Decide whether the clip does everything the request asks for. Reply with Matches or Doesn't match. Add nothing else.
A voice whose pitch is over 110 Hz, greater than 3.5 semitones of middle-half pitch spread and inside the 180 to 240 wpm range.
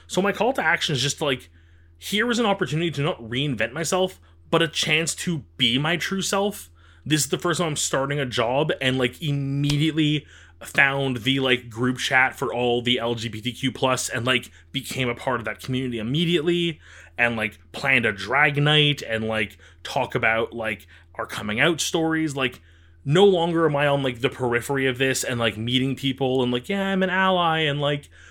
Matches